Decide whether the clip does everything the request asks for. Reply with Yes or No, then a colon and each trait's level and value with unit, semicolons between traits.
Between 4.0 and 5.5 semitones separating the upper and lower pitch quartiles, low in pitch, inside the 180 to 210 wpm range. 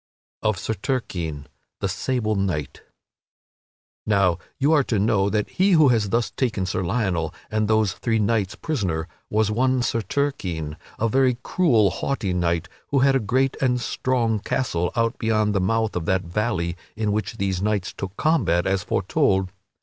No: average, 4.8 semitones; low, 105 Hz; average, 170 wpm